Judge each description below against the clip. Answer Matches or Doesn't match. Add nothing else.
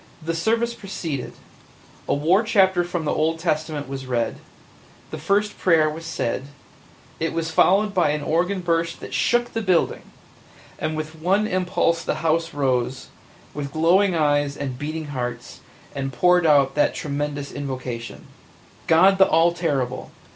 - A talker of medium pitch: Matches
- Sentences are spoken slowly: Doesn't match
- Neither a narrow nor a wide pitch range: Matches